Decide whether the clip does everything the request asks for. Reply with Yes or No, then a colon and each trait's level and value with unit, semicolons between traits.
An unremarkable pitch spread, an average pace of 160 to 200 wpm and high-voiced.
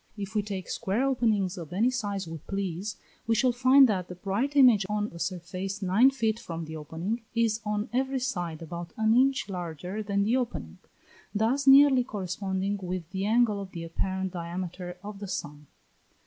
Yes: average, 4.3 semitones; average, 180 wpm; high, 200 Hz